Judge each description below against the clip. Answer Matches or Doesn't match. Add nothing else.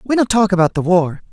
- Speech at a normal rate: Doesn't match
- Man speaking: Matches